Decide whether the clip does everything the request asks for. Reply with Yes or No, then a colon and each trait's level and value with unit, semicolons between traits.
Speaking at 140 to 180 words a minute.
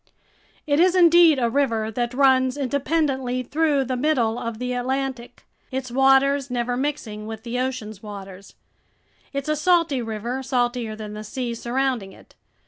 Yes: average, 150 wpm